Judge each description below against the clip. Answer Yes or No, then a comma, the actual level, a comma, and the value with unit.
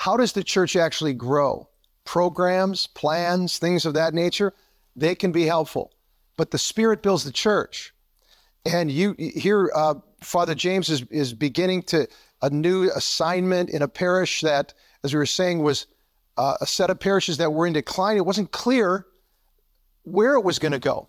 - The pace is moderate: Yes, average, 175 wpm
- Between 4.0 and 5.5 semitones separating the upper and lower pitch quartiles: No, average, 3.3 semitones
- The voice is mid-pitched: Yes, medium, 175 Hz